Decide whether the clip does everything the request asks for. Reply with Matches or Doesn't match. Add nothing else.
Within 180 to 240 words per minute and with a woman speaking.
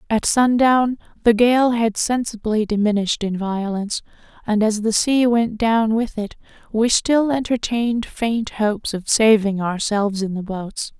Doesn't match